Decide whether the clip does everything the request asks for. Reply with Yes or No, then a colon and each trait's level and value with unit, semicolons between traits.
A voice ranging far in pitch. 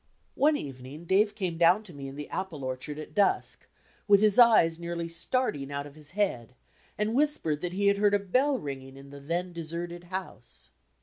Yes: wide, 6.1 semitones